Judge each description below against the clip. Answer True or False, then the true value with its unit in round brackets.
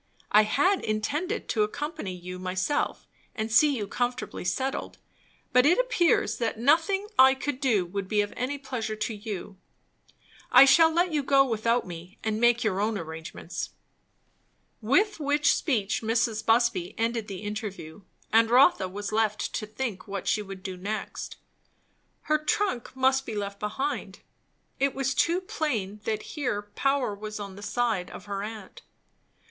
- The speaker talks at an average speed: True (160 wpm)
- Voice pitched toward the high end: True (225 Hz)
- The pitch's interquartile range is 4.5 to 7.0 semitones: True (4.9 semitones)